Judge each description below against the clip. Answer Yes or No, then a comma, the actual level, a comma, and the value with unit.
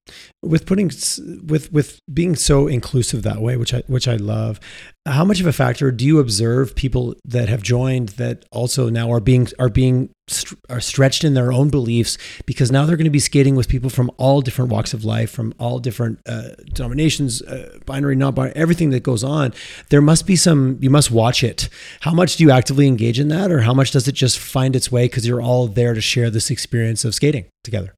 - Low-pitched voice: Yes, low, 130 Hz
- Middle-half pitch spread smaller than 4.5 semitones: Yes, average, 3.0 semitones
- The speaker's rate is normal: No, fast, 225 wpm